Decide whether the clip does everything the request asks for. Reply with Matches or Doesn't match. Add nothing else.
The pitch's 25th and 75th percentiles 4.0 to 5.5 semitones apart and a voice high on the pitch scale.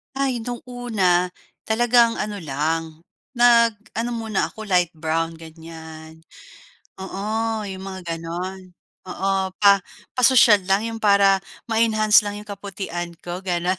Matches